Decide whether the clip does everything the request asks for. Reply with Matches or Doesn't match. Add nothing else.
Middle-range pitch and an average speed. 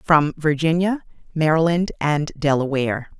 Doesn't match